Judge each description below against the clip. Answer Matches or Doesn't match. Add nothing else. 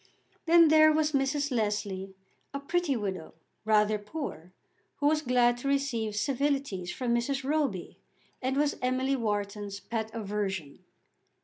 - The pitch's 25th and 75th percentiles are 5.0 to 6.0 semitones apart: Matches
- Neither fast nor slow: Doesn't match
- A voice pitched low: Doesn't match